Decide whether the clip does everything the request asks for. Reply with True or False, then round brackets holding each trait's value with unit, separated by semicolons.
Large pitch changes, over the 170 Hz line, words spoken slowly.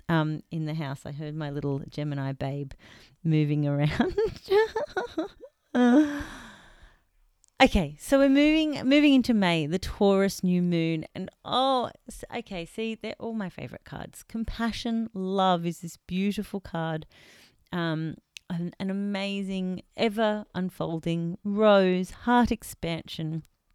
True (6.2 semitones; 185 Hz; 120 wpm)